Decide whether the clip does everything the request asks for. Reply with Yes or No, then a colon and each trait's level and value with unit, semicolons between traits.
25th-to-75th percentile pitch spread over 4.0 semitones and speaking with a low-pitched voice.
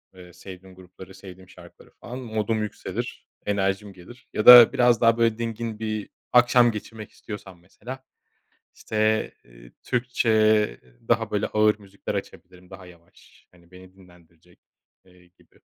No: average, 3.5 semitones; low, 105 Hz